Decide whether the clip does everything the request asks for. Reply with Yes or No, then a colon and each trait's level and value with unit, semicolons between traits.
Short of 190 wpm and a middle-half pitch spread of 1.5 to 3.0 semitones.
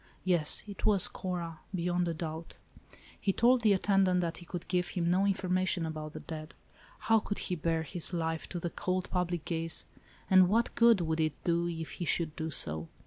No: average, 200 wpm; narrow, 2.4 semitones